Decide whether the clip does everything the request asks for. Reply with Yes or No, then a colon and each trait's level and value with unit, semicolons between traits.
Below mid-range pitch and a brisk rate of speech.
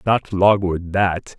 No: very low, 95 Hz; slow, 130 wpm